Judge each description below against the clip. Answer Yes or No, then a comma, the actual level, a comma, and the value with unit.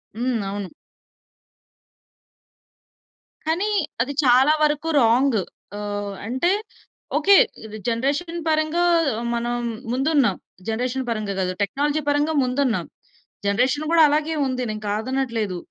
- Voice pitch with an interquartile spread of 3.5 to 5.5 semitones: Yes, average, 5.1 semitones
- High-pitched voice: Yes, very high, 255 Hz